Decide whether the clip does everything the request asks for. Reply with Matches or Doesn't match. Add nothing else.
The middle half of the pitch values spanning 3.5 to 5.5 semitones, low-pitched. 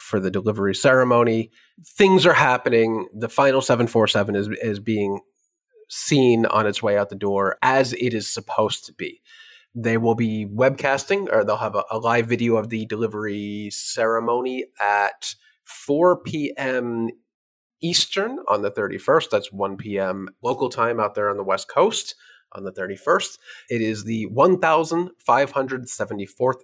Matches